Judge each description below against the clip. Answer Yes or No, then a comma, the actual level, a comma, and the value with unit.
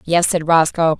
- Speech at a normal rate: Yes, average, 180 wpm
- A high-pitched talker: No, medium, 165 Hz